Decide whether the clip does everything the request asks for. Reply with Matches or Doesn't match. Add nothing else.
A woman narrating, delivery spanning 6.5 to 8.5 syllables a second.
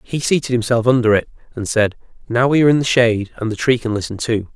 Doesn't match